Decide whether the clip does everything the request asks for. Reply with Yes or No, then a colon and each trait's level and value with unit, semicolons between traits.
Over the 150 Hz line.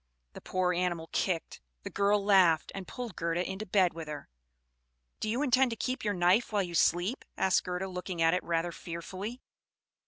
Yes: medium, 185 Hz